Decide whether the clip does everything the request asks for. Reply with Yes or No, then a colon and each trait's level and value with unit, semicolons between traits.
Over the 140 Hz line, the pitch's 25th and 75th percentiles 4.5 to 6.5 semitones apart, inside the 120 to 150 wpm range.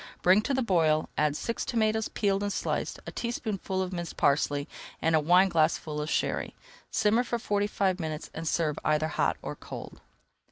No: medium, 185 Hz; average, 5.1 semitones; average, 175 wpm